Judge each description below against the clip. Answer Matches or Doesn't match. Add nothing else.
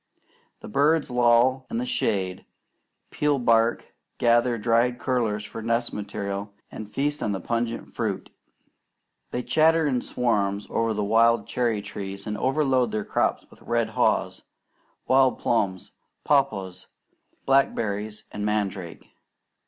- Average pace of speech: Doesn't match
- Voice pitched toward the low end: Matches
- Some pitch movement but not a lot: Matches